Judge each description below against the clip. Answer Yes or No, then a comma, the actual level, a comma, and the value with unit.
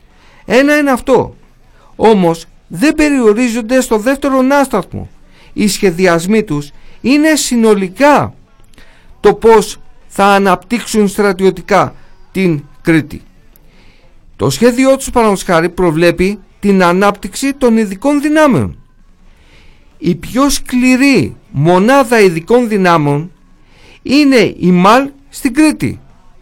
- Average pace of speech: No, slow, 95 wpm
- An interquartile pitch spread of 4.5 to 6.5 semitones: No, wide, 7.0 semitones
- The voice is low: No, high, 210 Hz